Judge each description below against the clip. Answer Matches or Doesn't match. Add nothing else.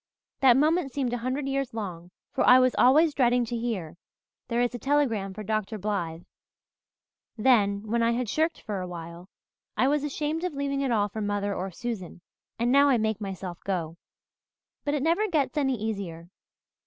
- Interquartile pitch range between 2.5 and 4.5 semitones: Doesn't match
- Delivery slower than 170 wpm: Doesn't match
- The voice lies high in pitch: Matches